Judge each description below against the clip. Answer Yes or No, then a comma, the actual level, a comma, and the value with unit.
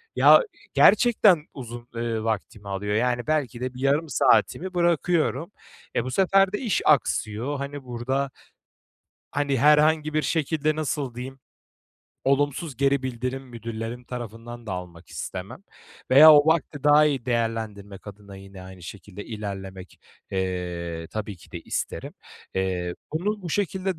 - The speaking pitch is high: No, low, 125 Hz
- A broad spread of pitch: Yes, wide, 6.5 semitones